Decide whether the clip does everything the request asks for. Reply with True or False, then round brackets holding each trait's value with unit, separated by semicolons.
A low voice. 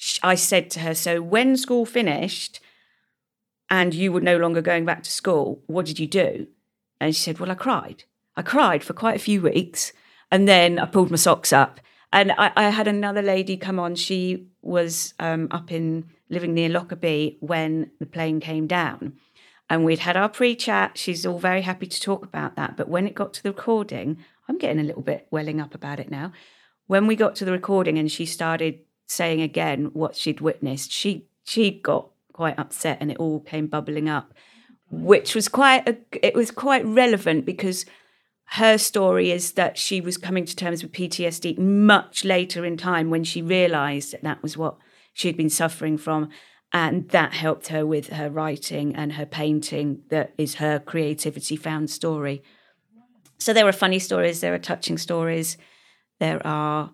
False (170 Hz)